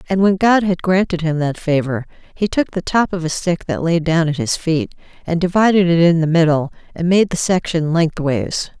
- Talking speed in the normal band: No, fast, 220 wpm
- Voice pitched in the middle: Yes, medium, 170 Hz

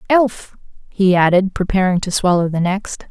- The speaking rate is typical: Yes, average, 155 wpm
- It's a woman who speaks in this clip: Yes, female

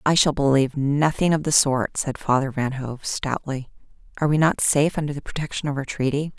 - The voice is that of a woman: Yes, female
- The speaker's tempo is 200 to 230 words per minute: Yes, fast, 205 wpm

